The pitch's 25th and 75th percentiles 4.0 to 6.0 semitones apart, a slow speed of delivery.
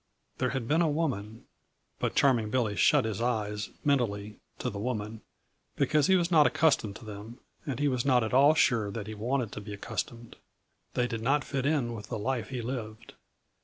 No: average, 4.3 semitones; average, 200 wpm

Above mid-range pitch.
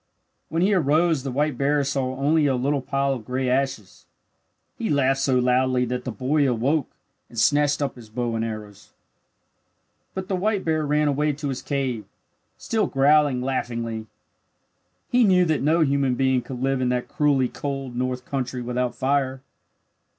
No: low, 135 Hz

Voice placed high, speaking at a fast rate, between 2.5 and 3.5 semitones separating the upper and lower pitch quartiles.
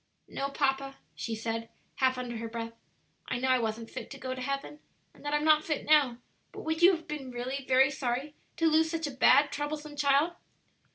Yes: very high, 275 Hz; fast, 210 wpm; average, 3.0 semitones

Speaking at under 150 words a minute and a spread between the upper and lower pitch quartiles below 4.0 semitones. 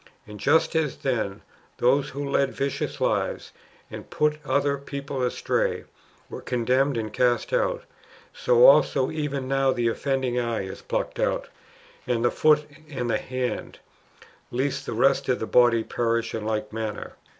No: average, 155 wpm; average, 3.2 semitones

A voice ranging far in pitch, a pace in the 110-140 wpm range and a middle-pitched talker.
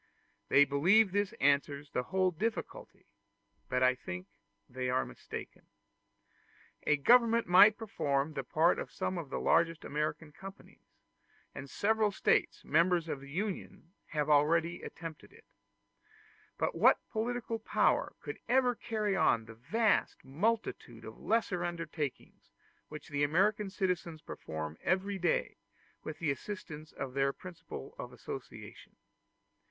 Yes: wide, 6.1 semitones; slow, 135 wpm; medium, 165 Hz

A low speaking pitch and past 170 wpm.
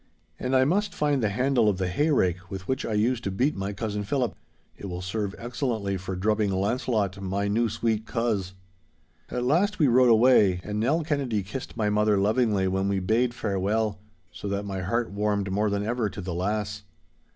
Yes: low, 105 Hz; average, 195 wpm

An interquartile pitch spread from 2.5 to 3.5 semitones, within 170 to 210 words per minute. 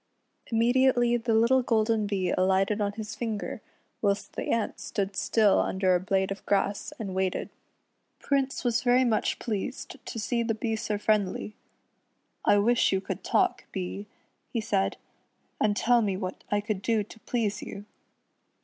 No: average, 2.9 semitones; average, 160 wpm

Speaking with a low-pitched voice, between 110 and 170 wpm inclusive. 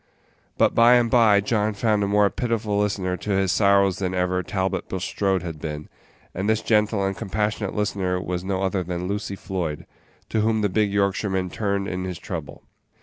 No: low, 100 Hz; average, 185 wpm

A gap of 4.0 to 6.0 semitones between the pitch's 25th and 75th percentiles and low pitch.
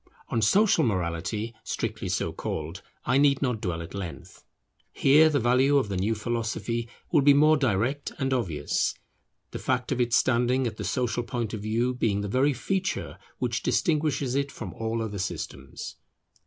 Yes: average, 4.6 semitones; low, 120 Hz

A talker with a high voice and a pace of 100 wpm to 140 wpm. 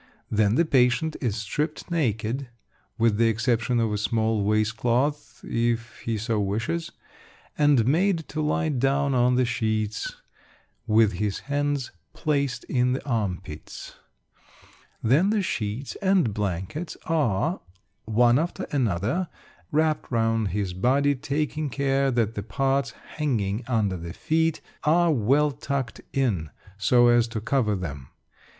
No: low, 120 Hz; slow, 135 wpm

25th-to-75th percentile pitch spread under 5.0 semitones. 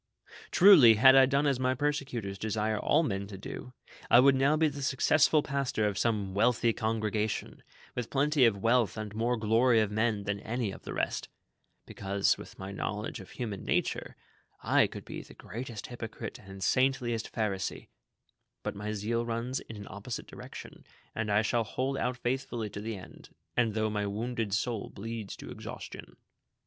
Yes: average, 3.4 semitones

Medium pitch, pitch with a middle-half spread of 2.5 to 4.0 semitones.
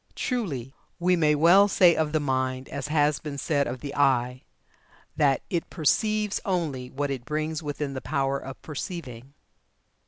Yes: medium, 145 Hz; average, 3.3 semitones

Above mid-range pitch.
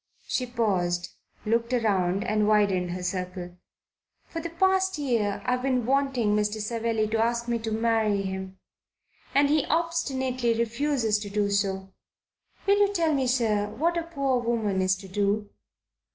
Yes: high, 225 Hz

